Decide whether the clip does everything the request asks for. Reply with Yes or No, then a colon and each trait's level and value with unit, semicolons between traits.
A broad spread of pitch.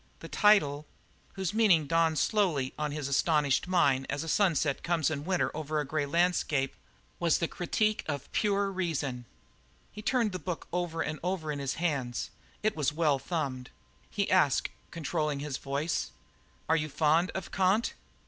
No: average, 4.0 semitones